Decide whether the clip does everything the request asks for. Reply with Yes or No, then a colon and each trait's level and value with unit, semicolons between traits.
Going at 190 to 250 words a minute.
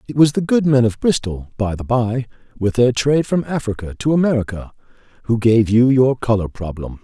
Yes: average, 195 wpm